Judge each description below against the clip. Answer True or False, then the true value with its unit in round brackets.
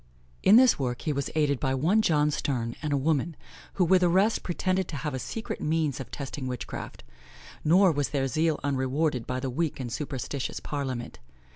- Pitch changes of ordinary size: True (3.9 semitones)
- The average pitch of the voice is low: False (145 Hz)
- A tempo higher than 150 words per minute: True (185 wpm)